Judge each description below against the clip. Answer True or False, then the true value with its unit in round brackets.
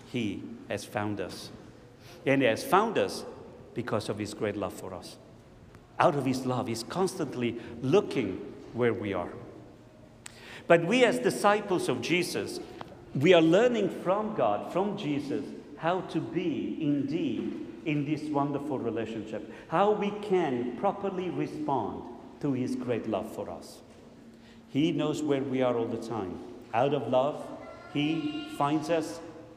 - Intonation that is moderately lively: False (7.2 semitones)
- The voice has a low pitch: False (150 Hz)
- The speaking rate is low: False (145 wpm)